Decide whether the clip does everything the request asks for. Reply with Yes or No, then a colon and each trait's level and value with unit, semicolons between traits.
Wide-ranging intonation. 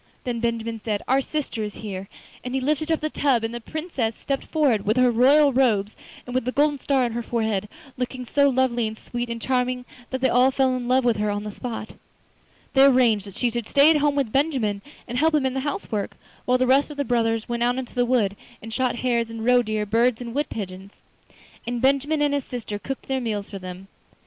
No: average, 3.2 semitones